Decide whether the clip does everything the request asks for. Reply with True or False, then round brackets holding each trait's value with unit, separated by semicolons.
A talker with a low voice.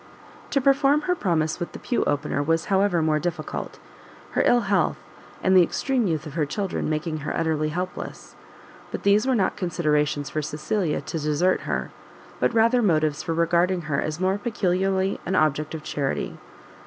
False (170 Hz)